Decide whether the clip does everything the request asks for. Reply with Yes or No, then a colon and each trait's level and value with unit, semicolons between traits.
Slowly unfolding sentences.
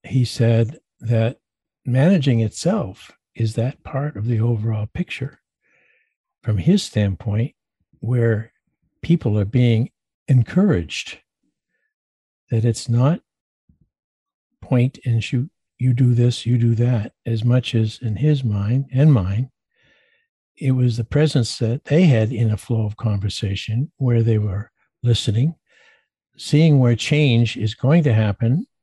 Yes: slow, 130 wpm